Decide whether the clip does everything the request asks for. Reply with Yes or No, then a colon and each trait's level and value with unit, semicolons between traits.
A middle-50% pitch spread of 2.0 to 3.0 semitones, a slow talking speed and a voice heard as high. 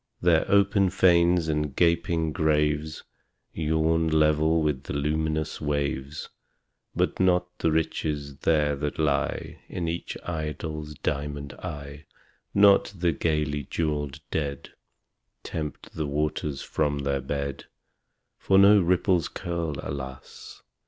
No: narrow, 2.4 semitones; slow, 115 wpm; very low, 75 Hz